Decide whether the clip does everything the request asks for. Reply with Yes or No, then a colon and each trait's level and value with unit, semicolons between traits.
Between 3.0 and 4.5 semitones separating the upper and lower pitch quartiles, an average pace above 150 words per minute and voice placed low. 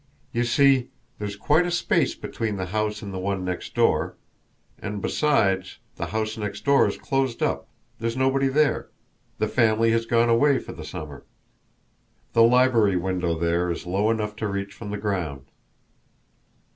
Yes: average, 3.9 semitones; average, 165 wpm; low, 110 Hz